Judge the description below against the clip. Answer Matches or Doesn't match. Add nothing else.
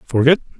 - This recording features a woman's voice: Doesn't match